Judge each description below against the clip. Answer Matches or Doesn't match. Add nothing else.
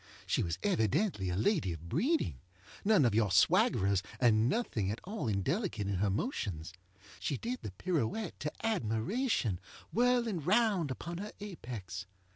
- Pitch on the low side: Matches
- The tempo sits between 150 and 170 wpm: Doesn't match